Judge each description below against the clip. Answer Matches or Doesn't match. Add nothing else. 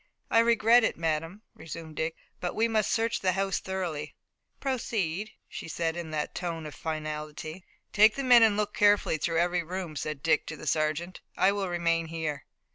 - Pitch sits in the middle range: Matches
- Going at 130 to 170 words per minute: Doesn't match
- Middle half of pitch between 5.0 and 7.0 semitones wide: Doesn't match